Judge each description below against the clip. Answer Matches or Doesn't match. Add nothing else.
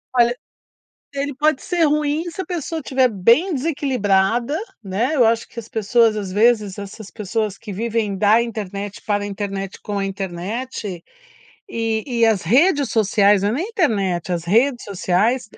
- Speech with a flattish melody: Doesn't match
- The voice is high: Matches